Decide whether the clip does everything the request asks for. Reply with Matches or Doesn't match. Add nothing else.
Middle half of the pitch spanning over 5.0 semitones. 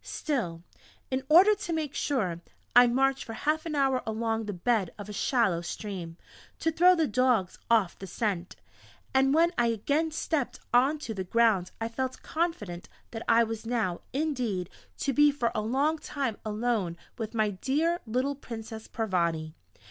Matches